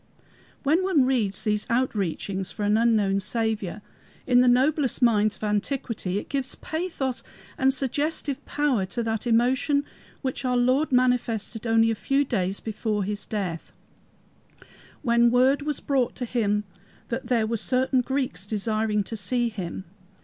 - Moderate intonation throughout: Yes, average, 3.9 semitones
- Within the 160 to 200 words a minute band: No, average, 145 wpm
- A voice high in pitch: Yes, high, 235 Hz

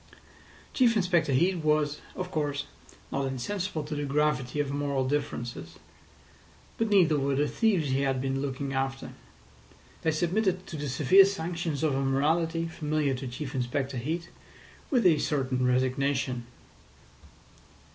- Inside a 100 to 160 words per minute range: Yes, average, 140 wpm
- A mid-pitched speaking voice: Yes, medium, 145 Hz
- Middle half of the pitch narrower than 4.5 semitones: Yes, average, 3.8 semitones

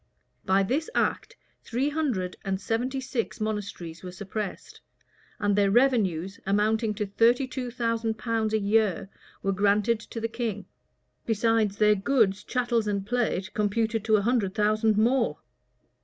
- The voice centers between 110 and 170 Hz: No, high, 215 Hz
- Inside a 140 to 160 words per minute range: Yes, average, 150 wpm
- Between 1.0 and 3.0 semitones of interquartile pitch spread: Yes, narrow, 2.6 semitones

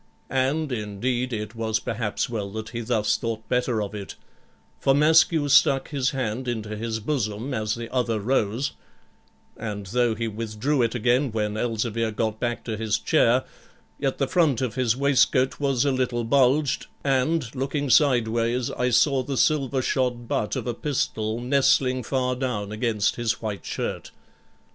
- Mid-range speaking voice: No, low, 120 Hz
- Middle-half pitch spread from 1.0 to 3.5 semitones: Yes, average, 3.2 semitones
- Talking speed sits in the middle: Yes, average, 160 wpm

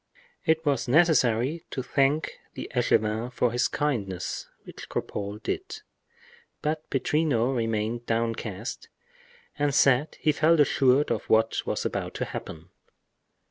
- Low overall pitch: Yes, low, 125 Hz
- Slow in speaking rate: Yes, slow, 125 wpm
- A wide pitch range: No, average, 4.8 semitones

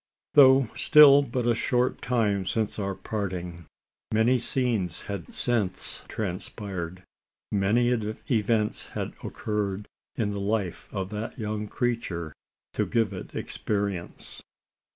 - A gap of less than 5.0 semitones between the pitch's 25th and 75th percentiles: Yes, average, 3.6 semitones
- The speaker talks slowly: Yes, slow, 115 wpm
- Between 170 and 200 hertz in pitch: No, low, 105 Hz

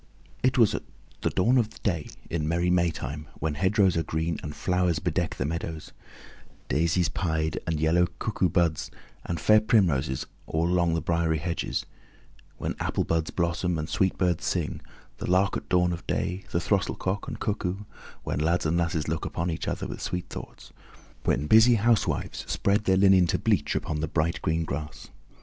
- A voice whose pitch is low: Yes, very low, 85 Hz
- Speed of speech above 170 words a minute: Yes, average, 180 wpm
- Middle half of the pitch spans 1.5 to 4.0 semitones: Yes, narrow, 2.6 semitones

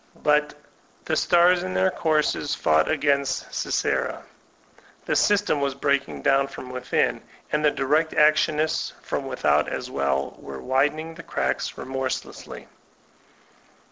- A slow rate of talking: Yes, slow, 130 wpm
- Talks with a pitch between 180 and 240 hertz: No, medium, 140 Hz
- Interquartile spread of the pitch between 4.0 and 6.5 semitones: No, average, 3.0 semitones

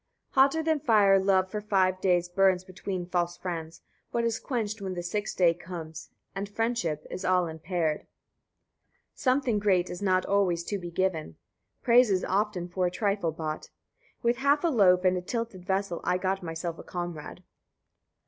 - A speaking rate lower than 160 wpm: No, average, 175 wpm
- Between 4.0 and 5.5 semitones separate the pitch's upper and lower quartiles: No, average, 3.1 semitones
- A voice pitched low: No, medium, 185 Hz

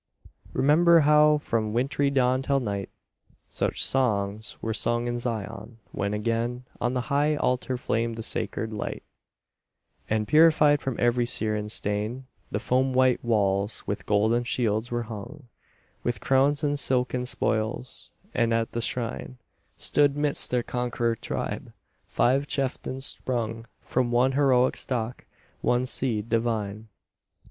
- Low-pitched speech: Yes, low, 120 Hz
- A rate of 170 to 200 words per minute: No, slow, 135 wpm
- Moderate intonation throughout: Yes, average, 3.0 semitones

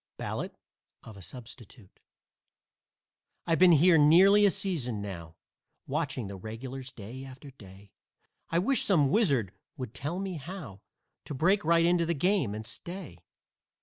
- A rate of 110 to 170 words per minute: Yes, average, 145 wpm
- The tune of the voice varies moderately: No, wide, 7.9 semitones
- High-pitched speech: No, medium, 140 Hz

